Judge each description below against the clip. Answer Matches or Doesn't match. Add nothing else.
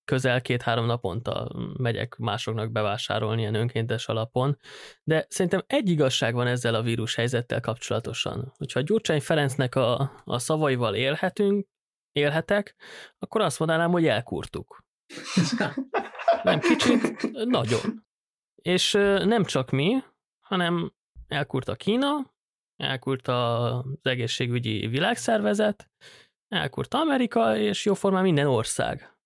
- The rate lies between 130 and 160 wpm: Doesn't match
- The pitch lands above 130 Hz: Matches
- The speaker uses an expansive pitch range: Matches